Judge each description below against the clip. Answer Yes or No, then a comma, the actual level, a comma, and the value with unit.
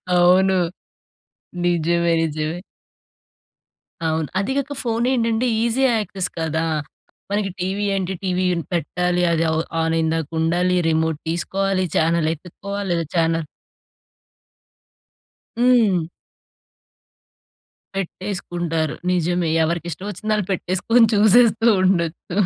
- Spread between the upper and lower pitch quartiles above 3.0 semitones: Yes, average, 3.5 semitones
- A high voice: No, medium, 180 Hz